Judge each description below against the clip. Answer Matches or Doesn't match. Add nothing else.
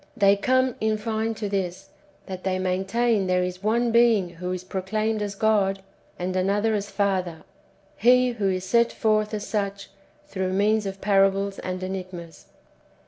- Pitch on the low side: Doesn't match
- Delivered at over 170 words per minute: Doesn't match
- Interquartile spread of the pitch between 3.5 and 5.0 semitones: Doesn't match